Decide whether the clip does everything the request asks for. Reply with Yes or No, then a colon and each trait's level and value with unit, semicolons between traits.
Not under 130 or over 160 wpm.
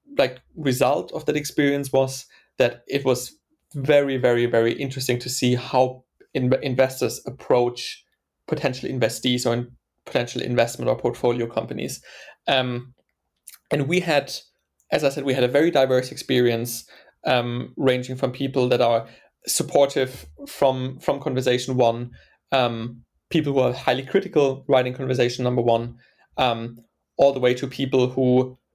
Yes: average, 145 wpm